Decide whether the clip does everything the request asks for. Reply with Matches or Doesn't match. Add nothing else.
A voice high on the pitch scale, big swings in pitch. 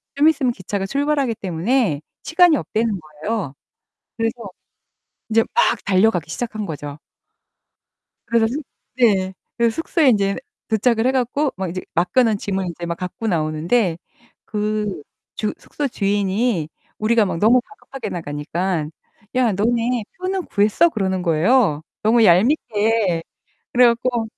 Doesn't match